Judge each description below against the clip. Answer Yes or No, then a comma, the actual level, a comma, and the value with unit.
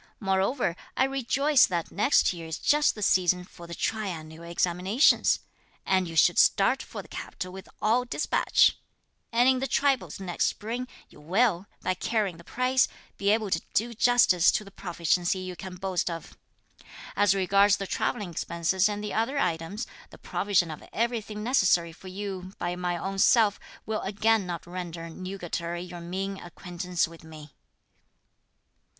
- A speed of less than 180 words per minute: Yes, average, 160 wpm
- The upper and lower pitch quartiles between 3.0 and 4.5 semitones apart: Yes, average, 3.8 semitones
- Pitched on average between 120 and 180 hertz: No, high, 190 Hz